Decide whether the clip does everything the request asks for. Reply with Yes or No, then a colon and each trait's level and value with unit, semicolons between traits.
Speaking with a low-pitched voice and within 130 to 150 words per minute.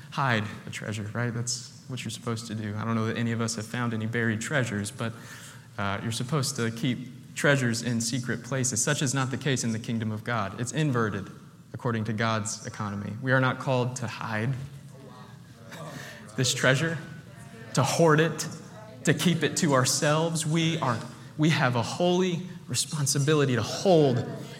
No: low, 130 Hz; average, 180 wpm